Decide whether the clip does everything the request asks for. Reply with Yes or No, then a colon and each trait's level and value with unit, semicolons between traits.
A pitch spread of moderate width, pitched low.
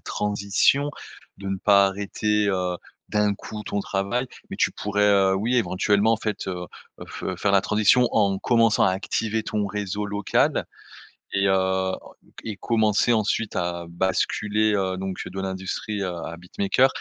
No: narrow, 1.9 semitones; low, 100 Hz